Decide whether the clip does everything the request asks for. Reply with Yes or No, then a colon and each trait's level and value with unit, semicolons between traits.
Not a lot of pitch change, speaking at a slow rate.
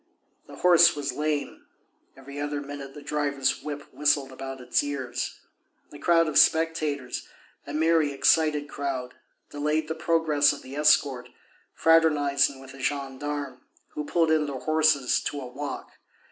No: narrow, 2.0 semitones; average, 145 wpm